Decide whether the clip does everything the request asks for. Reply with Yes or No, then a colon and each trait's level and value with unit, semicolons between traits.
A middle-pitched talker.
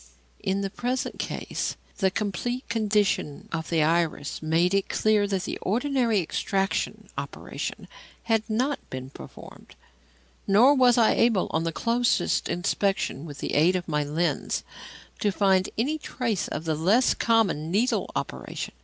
No: high, 195 Hz